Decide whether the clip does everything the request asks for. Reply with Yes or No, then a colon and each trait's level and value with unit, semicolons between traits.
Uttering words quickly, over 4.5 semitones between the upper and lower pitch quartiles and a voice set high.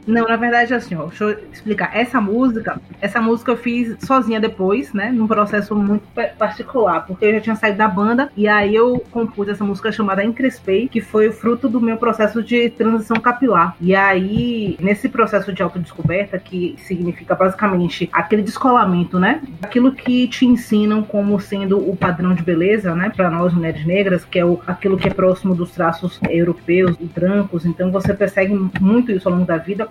No: fast, 190 wpm; average, 3.6 semitones; high, 205 Hz